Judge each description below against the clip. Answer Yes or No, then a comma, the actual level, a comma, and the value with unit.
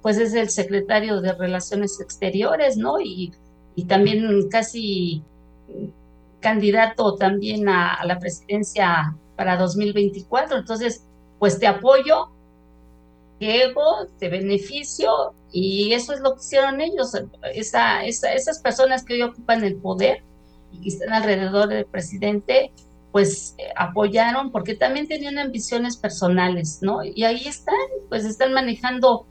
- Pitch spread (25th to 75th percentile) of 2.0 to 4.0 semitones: No, average, 4.7 semitones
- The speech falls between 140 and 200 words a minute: No, average, 130 wpm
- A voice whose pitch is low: No, high, 205 Hz